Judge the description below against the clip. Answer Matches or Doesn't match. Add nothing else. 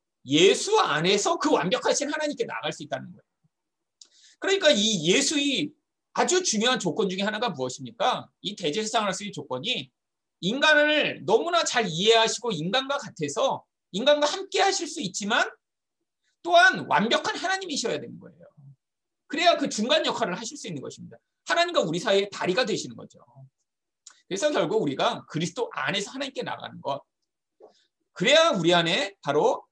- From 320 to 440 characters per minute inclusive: Matches